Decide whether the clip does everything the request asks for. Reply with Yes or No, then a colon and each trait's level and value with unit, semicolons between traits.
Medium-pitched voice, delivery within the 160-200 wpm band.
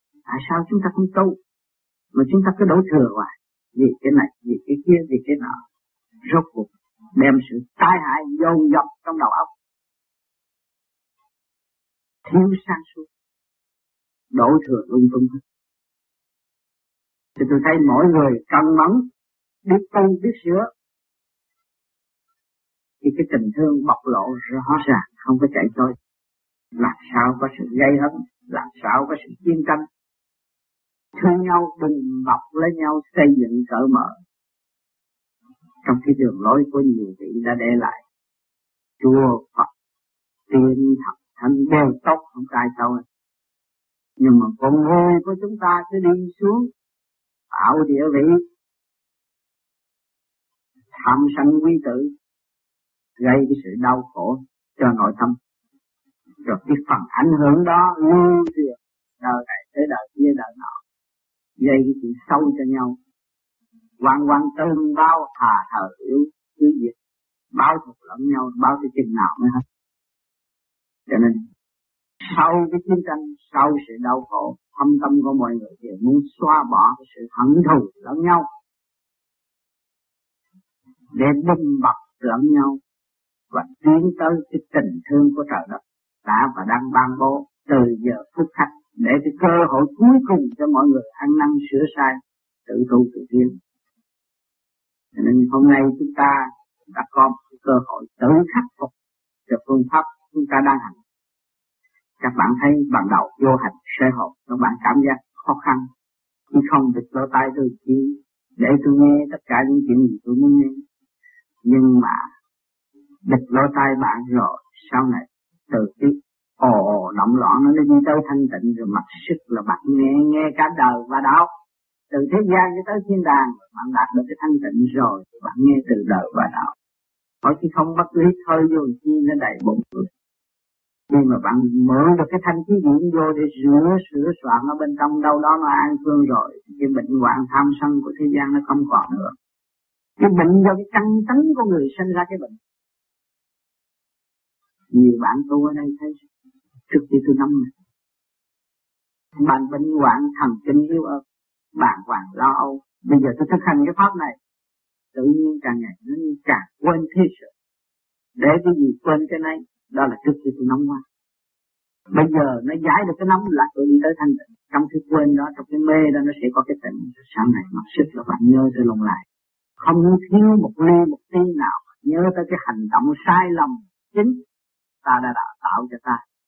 Yes: medium, 175 Hz; average, 170 wpm